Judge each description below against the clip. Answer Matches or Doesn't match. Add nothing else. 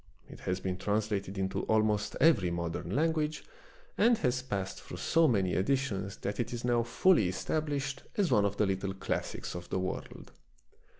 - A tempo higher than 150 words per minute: Matches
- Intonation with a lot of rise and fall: Matches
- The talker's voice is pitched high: Doesn't match